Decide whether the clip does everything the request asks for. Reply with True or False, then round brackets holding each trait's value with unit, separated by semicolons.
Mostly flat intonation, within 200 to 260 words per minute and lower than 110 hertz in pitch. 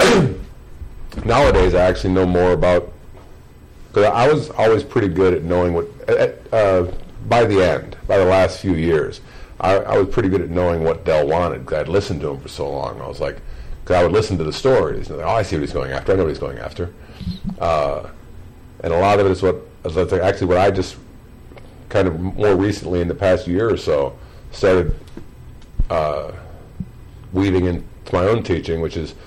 True (2.3 semitones; 205 wpm; 90 Hz)